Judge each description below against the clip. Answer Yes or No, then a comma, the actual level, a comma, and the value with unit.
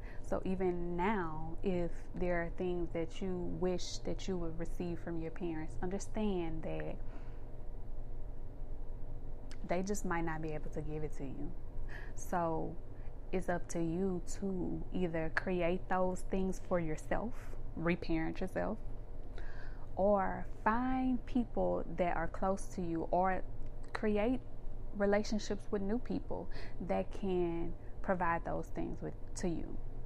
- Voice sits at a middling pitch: Yes, medium, 170 Hz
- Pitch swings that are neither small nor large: No, wide, 7.7 semitones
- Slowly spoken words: Yes, slow, 130 wpm